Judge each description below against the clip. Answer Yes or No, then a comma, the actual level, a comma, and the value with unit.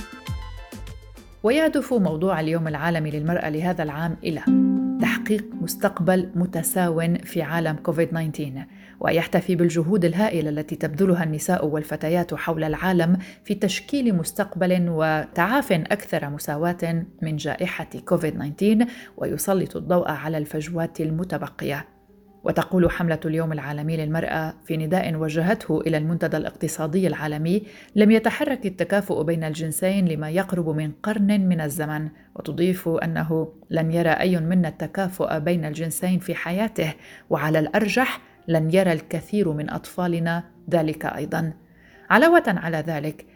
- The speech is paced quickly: No, average, 120 wpm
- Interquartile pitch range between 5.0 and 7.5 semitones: No, average, 2.9 semitones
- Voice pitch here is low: No, medium, 165 Hz